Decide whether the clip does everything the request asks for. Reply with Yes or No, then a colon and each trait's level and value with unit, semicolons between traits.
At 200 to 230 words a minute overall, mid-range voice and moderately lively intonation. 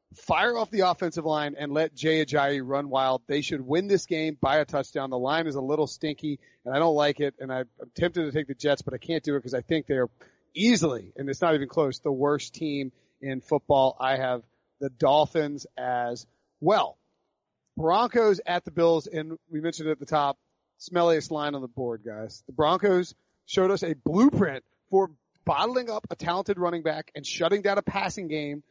Yes: fast, 205 wpm; medium, 155 Hz; average, 3.7 semitones